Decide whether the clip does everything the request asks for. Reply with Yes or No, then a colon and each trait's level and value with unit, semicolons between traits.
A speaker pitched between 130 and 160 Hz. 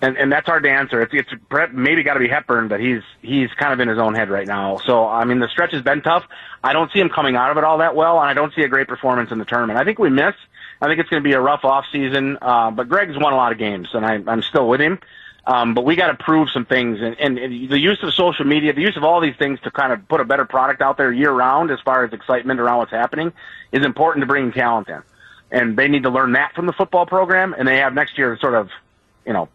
Yes: low, 135 Hz